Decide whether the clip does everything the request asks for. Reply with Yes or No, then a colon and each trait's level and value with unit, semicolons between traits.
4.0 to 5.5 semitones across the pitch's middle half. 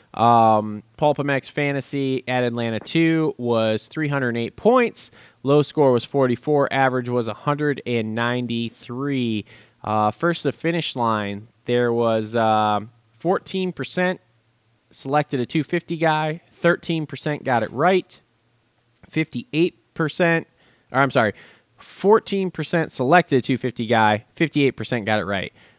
Yes: average, 5.2 semitones